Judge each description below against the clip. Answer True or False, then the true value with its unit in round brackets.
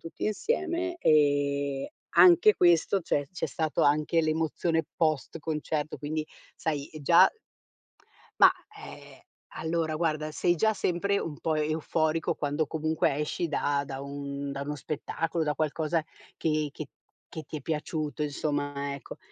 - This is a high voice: False (155 Hz)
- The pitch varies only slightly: True (2.2 semitones)